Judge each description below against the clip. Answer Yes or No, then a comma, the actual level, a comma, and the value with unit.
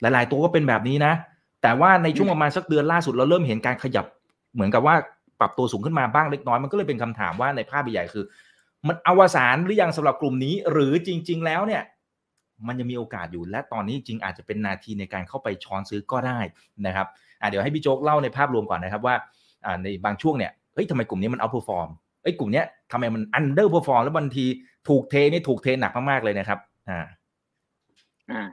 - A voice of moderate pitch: No, low, 130 Hz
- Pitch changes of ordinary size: No, wide, 6.1 semitones